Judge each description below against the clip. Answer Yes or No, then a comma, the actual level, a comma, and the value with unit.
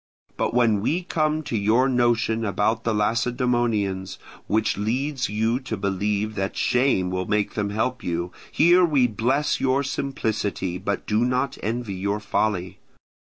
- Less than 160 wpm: Yes, average, 150 wpm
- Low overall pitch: Yes, low, 110 Hz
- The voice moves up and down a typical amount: Yes, average, 3.8 semitones